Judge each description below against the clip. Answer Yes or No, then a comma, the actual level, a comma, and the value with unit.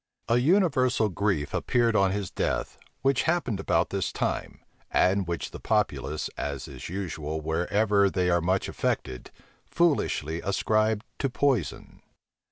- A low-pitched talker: Yes, low, 100 Hz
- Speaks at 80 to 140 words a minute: Yes, slow, 135 wpm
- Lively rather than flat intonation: Yes, wide, 5.9 semitones